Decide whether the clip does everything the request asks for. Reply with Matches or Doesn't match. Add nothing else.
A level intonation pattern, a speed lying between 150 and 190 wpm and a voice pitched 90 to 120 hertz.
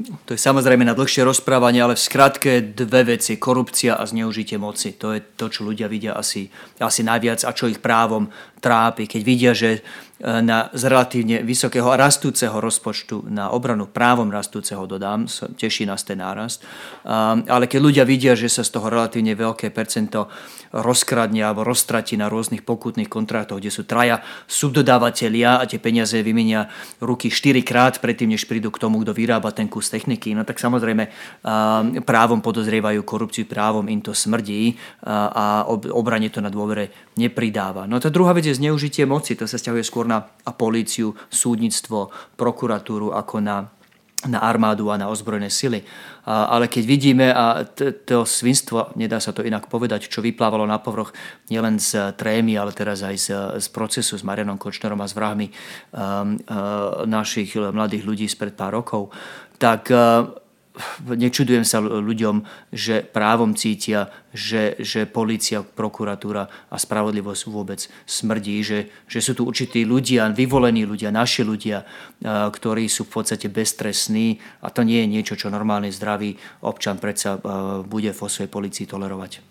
Matches